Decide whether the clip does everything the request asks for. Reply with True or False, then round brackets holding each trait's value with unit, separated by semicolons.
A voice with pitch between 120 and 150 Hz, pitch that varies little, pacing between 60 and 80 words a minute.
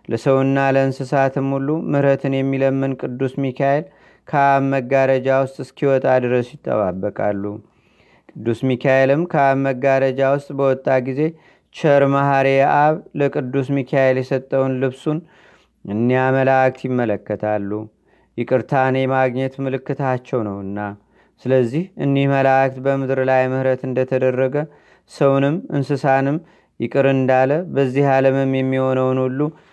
False (135 Hz; 1.1 semitones; 95 wpm)